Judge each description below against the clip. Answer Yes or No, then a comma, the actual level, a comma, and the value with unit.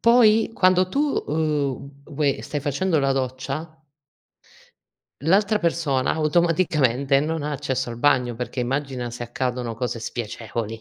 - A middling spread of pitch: Yes, average, 4.3 semitones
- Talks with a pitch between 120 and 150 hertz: Yes, medium, 140 Hz